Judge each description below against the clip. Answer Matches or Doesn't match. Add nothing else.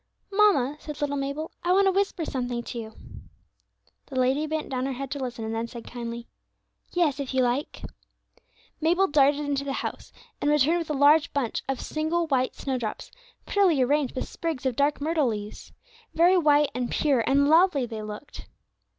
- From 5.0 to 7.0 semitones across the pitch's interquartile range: Doesn't match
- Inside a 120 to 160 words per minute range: Doesn't match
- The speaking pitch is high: Matches